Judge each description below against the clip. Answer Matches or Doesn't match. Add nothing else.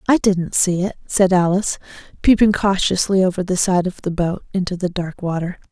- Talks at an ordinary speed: Matches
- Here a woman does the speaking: Matches